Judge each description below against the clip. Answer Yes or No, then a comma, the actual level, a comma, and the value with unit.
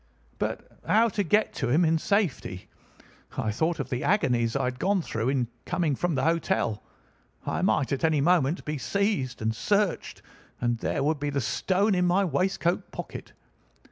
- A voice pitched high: No, medium, 160 Hz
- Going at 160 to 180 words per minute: Yes, average, 175 wpm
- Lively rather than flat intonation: Yes, wide, 6.5 semitones